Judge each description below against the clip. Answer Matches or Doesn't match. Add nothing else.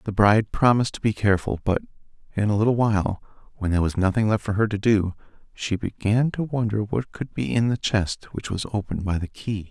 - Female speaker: Doesn't match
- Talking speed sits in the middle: Doesn't match